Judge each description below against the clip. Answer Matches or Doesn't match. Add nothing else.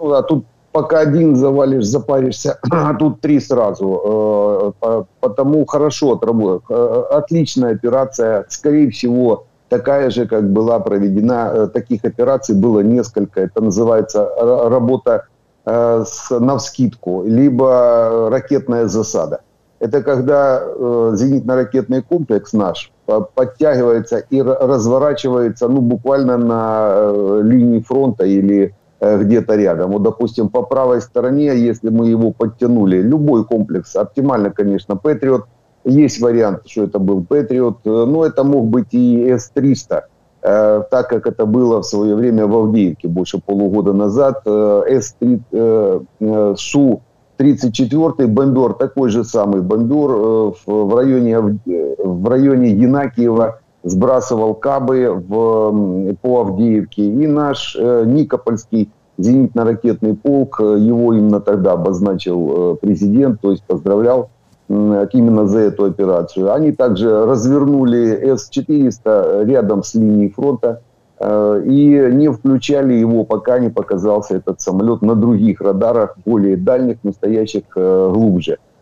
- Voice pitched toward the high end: Doesn't match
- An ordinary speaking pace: Matches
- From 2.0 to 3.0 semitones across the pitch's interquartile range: Doesn't match